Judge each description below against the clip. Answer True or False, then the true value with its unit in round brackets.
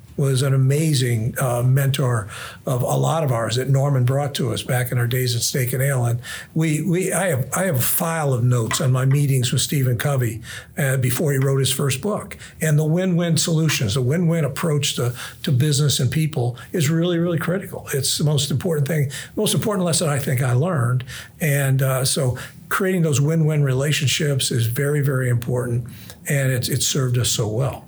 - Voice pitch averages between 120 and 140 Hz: True (135 Hz)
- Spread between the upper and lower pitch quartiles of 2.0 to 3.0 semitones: False (3.4 semitones)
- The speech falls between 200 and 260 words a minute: True (205 wpm)